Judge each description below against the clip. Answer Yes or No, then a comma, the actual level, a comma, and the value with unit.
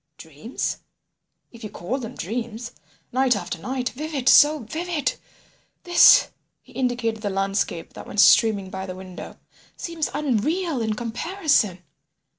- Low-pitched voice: No, high, 235 Hz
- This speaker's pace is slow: Yes, slow, 125 wpm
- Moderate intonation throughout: No, wide, 5.7 semitones